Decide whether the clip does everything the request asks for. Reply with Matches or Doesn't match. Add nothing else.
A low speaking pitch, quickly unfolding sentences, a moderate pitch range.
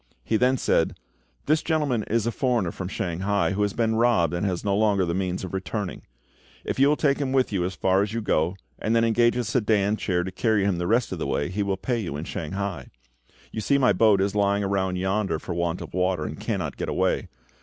Matches